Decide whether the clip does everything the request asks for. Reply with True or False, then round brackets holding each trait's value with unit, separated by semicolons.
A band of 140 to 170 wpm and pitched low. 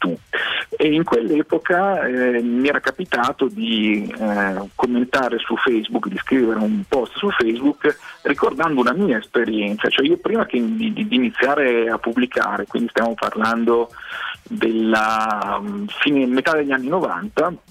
False (130 wpm; 125 Hz)